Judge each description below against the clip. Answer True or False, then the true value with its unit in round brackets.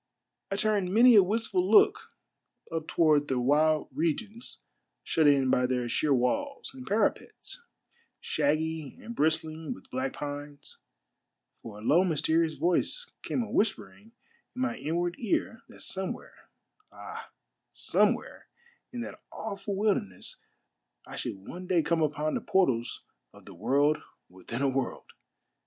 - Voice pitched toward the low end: False (160 Hz)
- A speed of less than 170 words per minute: True (145 wpm)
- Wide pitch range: True (6.6 semitones)